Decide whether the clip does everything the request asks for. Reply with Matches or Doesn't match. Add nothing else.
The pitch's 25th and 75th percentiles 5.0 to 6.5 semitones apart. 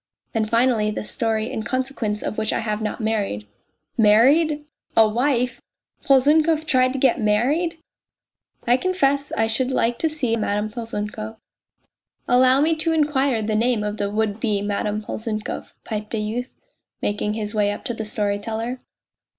Doesn't match